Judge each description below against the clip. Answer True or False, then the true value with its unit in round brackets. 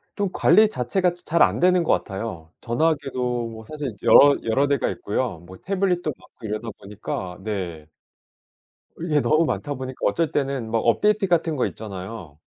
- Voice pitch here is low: True (130 Hz)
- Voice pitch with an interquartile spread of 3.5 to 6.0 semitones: False (7.3 semitones)